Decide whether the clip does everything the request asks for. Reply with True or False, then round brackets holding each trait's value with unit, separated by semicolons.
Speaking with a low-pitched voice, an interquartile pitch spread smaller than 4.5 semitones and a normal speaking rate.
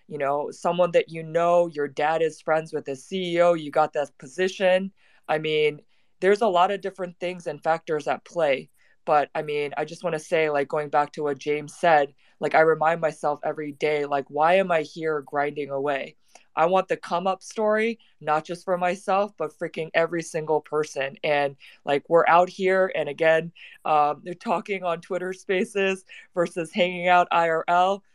False (160 Hz; 3.2 semitones; 190 wpm)